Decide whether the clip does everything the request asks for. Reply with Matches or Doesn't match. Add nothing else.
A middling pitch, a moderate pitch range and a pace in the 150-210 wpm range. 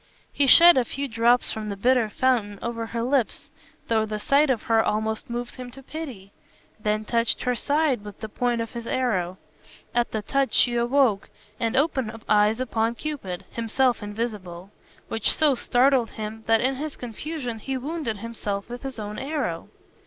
Doesn't match